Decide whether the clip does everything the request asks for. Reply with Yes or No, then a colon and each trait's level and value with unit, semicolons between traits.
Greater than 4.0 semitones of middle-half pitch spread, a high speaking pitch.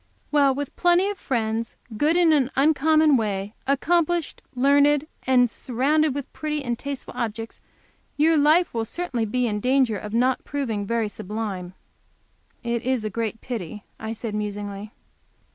Yes: average, 5.1 semitones; very high, 250 Hz